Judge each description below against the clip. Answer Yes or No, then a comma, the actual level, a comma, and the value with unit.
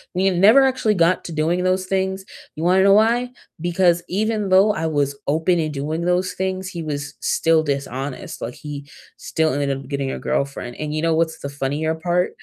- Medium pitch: Yes, medium, 165 Hz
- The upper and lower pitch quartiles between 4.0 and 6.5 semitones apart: Yes, average, 4.5 semitones